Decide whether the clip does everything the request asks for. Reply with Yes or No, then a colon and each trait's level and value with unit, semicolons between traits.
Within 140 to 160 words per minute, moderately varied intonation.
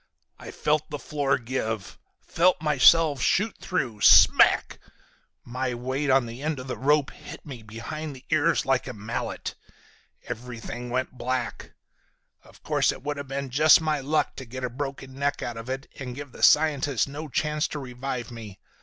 No: average, 175 wpm; average, 3.2 semitones